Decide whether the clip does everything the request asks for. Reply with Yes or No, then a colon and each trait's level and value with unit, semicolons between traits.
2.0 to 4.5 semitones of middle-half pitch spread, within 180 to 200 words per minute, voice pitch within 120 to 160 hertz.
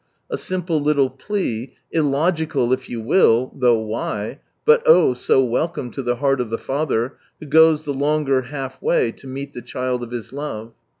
Yes: average, 3.9 semitones; average, 190 wpm; low, 135 Hz